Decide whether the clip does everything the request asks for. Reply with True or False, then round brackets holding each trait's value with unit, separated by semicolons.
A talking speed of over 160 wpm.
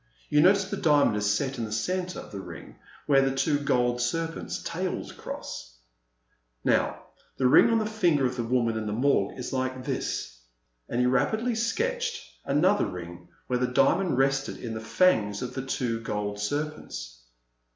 True (175 wpm)